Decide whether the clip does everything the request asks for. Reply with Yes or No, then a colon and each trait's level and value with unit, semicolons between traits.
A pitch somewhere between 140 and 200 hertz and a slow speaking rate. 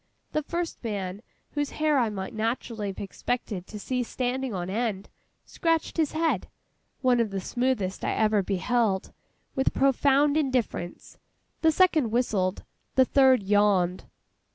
No: high, 240 Hz; slow, 130 wpm